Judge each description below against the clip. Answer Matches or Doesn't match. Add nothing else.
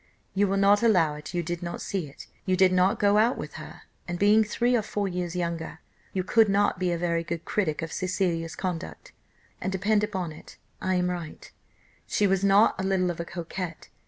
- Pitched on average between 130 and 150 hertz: Doesn't match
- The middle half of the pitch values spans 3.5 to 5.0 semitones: Doesn't match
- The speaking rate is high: Matches